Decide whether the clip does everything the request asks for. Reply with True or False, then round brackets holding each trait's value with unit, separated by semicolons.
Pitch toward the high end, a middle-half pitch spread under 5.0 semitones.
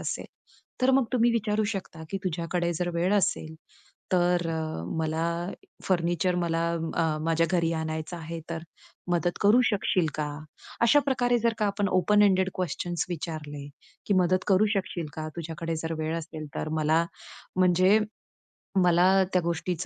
False (175 Hz; 2.8 semitones)